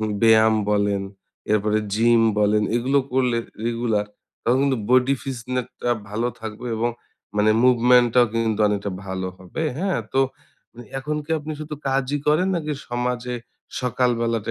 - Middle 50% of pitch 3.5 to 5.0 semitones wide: No, average, 2.9 semitones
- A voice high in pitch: No, low, 120 Hz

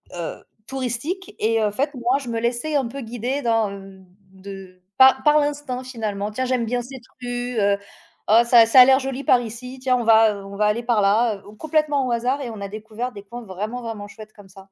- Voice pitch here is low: No, high, 235 Hz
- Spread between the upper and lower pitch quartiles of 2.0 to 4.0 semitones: Yes, average, 3.4 semitones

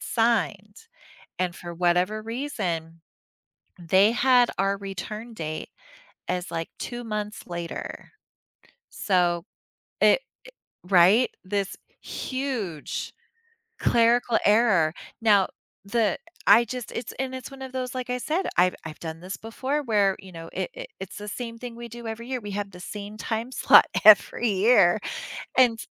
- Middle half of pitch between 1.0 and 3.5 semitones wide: No, average, 4.7 semitones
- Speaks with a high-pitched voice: Yes, high, 210 Hz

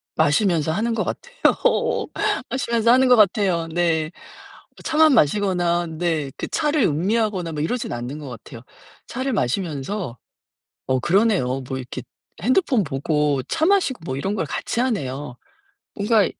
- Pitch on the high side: No, medium, 175 Hz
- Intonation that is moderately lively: No, wide, 7.7 semitones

